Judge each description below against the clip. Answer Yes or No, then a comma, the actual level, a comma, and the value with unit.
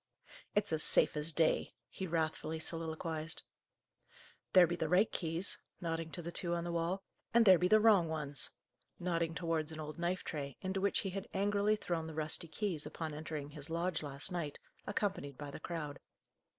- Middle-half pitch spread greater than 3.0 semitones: No, average, 2.7 semitones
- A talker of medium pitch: Yes, medium, 165 Hz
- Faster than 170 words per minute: Yes, average, 185 wpm